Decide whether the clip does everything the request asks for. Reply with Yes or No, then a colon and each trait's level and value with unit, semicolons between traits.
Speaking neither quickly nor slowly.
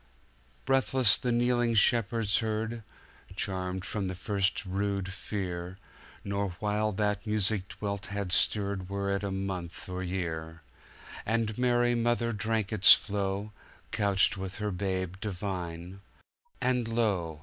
No: slow, 115 wpm